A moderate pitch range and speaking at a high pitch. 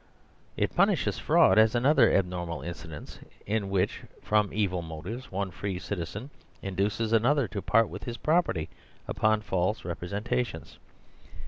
No: average, 4.0 semitones; low, 100 Hz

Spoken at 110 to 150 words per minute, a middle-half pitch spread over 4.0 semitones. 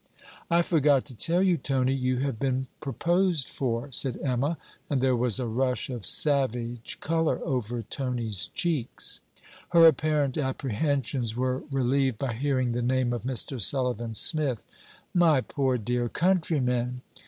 No: average, 140 wpm; average, 2.9 semitones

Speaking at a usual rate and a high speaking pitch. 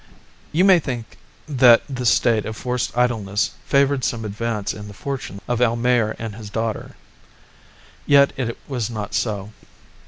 No: average, 150 wpm; low, 115 Hz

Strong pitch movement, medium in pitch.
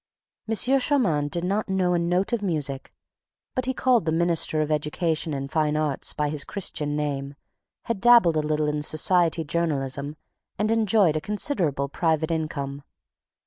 No: average, 4.4 semitones; medium, 160 Hz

